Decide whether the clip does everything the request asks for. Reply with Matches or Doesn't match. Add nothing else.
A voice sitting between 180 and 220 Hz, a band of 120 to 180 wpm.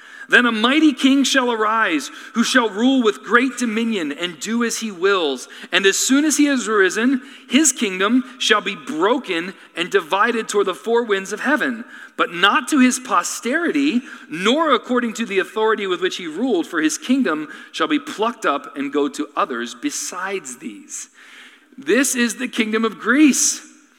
Doesn't match